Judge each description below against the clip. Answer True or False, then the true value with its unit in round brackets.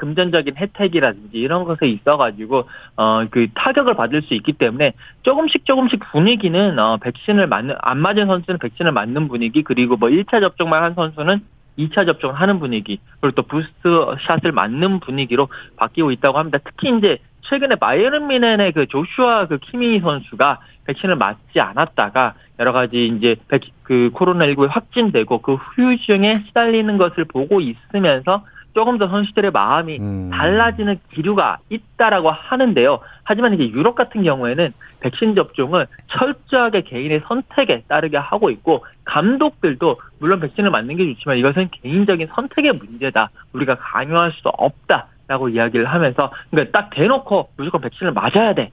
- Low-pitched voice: False (170 Hz)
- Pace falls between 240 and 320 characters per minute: False (365 characters per minute)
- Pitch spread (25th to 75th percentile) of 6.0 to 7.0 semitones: False (7.7 semitones)